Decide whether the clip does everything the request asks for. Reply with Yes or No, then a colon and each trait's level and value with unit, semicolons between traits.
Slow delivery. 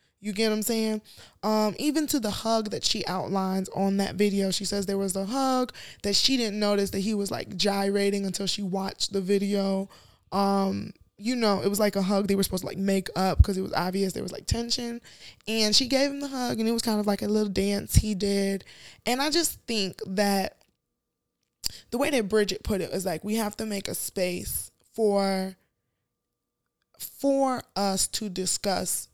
No: fast, 205 wpm